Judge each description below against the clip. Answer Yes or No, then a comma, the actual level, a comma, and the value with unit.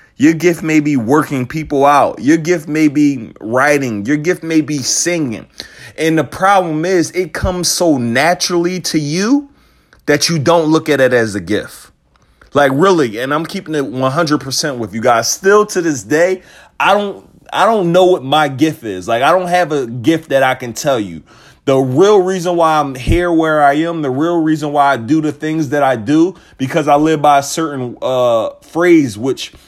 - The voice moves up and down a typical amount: Yes, average, 3.8 semitones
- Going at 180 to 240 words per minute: Yes, average, 200 wpm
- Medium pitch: Yes, medium, 155 Hz